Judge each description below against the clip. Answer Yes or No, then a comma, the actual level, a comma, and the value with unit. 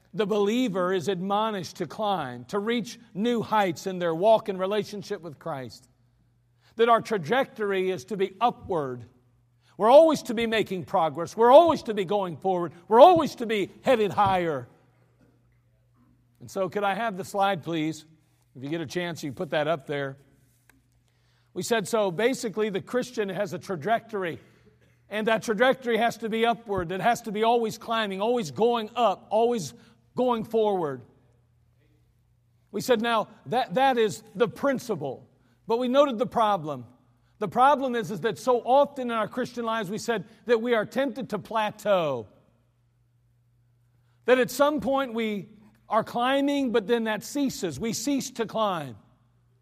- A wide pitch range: Yes, wide, 8.9 semitones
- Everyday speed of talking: Yes, average, 165 wpm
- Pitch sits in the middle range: No, high, 205 Hz